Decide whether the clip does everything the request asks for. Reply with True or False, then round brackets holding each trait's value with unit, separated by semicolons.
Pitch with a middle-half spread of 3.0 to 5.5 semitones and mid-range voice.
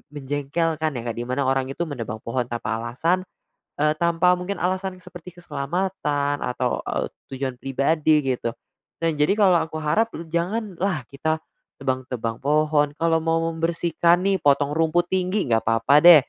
True (4.2 semitones; 155 Hz)